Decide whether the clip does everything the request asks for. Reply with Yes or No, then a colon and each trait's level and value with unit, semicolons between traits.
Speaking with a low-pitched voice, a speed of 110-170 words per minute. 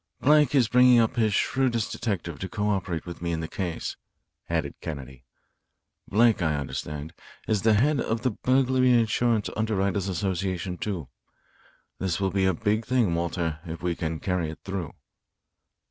Yes: very low, 95 Hz; average, 160 wpm